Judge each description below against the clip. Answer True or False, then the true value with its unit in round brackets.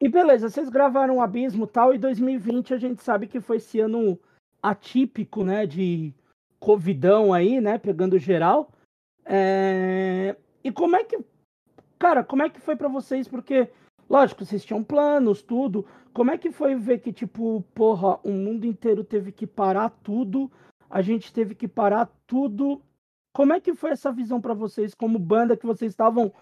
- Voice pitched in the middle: False (230 Hz)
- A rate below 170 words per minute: False (175 wpm)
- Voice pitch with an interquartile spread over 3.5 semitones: True (4.1 semitones)